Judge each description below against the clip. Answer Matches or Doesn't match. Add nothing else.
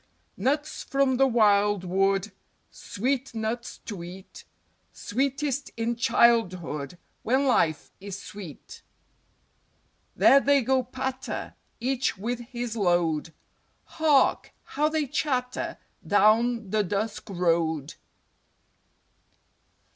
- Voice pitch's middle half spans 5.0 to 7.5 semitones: Matches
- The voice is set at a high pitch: Matches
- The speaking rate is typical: Doesn't match